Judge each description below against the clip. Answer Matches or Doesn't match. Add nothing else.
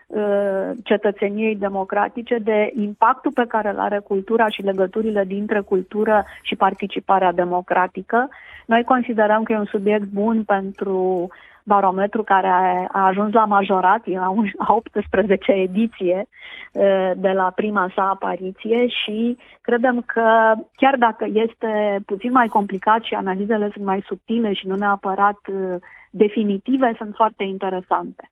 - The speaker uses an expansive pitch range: Doesn't match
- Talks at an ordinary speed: Matches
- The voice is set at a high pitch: Matches